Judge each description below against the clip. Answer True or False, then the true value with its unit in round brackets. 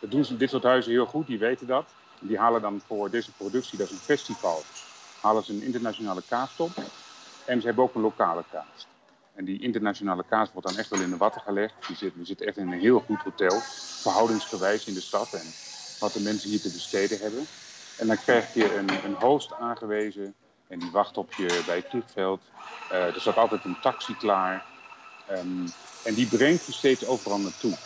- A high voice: False (105 Hz)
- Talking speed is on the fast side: True (210 wpm)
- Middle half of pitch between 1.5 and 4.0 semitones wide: True (3.6 semitones)